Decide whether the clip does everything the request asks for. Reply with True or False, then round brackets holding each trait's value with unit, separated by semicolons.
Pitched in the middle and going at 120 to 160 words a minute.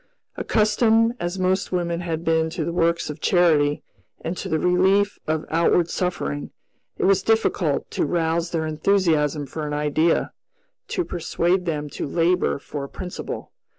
True (170 Hz; 150 wpm)